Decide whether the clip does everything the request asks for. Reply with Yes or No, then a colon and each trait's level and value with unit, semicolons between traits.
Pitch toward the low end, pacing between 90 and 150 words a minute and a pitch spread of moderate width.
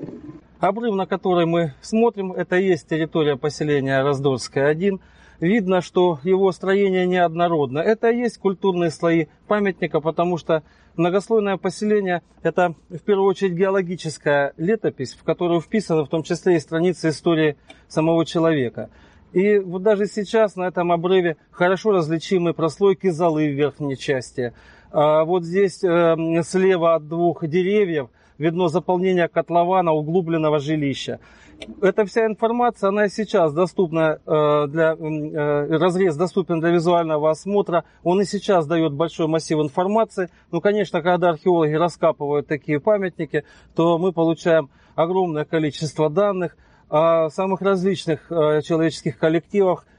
No: medium, 170 Hz; average, 130 wpm; average, 3.3 semitones